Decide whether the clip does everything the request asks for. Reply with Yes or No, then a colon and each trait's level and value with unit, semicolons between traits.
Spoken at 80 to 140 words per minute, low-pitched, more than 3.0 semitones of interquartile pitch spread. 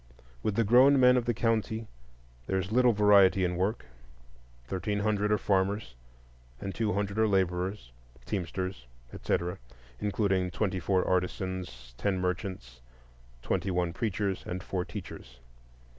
No: slow, 135 wpm; very low, 95 Hz; narrow, 2.6 semitones